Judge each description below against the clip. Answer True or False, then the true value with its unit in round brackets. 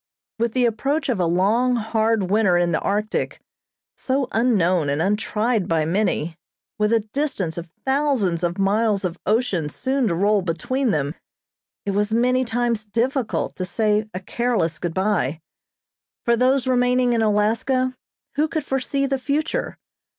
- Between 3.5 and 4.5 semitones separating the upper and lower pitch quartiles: False (5.2 semitones)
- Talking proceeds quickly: False (155 wpm)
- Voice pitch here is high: True (220 Hz)